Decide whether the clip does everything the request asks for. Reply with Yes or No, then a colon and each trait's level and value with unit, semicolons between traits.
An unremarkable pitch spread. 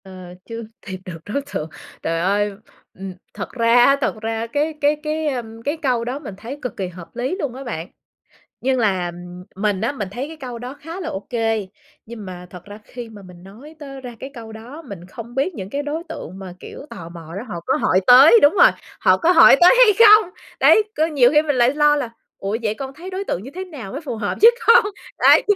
No: wide, 6.7 semitones